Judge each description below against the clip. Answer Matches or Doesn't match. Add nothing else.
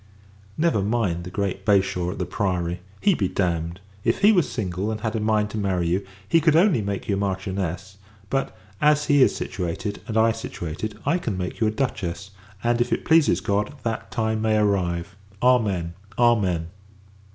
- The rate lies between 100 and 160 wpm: Doesn't match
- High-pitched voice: Doesn't match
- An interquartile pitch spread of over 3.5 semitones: Matches